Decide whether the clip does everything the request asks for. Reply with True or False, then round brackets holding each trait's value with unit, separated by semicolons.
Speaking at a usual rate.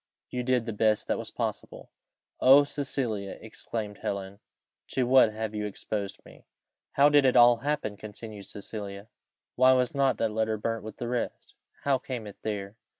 True (170 wpm)